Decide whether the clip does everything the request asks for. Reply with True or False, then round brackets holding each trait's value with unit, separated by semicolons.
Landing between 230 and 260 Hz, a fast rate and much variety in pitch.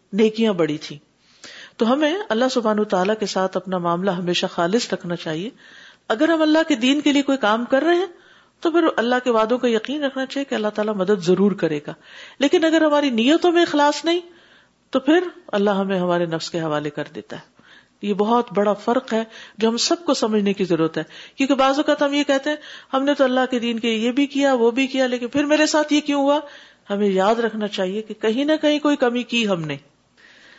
True (235 Hz; 225 wpm; 6.4 semitones)